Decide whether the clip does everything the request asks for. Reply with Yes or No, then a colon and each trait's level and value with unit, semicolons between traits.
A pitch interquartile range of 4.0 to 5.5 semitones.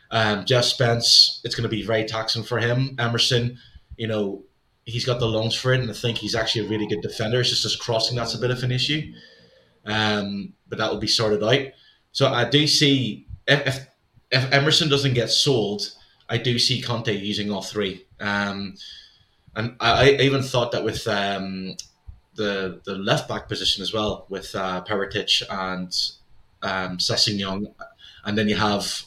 No: average, 3.2 semitones